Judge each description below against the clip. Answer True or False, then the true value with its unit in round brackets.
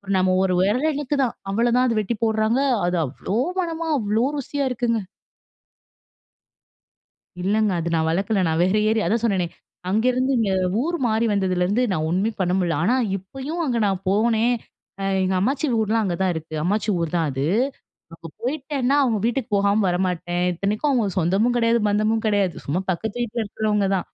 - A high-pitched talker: True (215 Hz)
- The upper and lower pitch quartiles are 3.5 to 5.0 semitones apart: True (4.3 semitones)